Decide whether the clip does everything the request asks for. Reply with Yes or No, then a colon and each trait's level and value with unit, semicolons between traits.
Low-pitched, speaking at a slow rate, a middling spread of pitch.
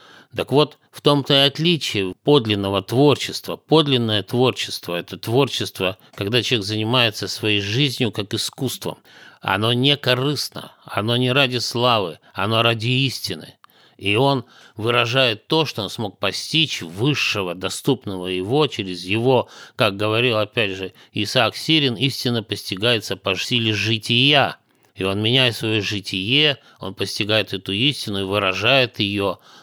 No: low, 115 Hz; average, 130 wpm; average, 4.5 semitones